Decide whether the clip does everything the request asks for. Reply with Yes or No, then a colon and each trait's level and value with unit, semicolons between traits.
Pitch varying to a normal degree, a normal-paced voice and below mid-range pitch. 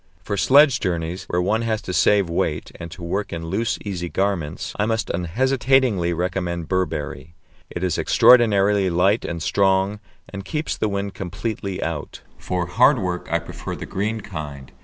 Yes: average, 3.5 semitones; average, 165 wpm; very low, 95 Hz